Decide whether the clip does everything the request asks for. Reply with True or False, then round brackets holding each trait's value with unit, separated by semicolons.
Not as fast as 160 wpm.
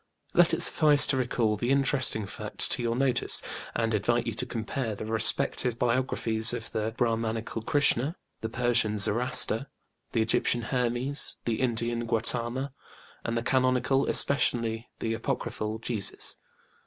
True (140 wpm)